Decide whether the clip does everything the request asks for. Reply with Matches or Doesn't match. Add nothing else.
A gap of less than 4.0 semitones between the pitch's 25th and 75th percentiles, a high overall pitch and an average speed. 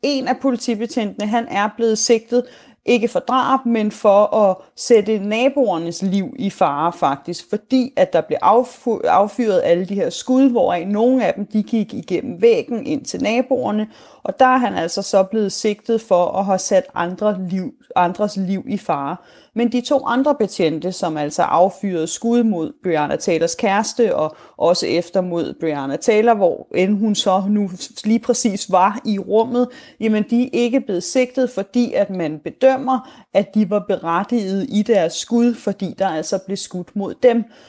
Doesn't match